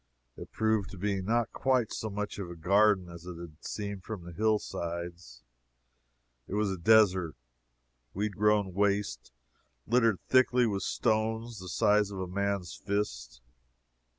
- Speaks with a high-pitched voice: No, low, 100 Hz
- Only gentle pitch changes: No, average, 3.4 semitones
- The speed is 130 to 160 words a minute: Yes, average, 150 wpm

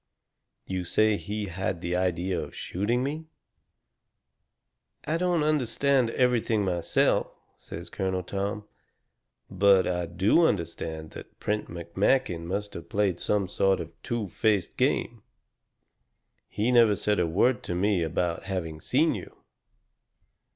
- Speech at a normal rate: No, slow, 130 wpm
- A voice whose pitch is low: Yes, very low, 95 Hz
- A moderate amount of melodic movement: Yes, average, 4.0 semitones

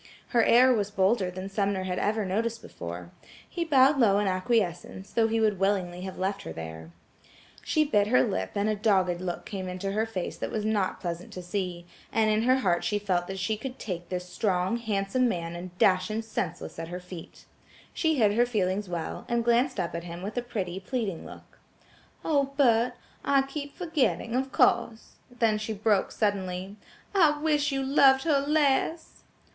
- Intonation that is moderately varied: Yes, average, 4.9 semitones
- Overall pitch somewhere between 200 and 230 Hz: Yes, high, 205 Hz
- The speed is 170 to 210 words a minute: Yes, average, 190 wpm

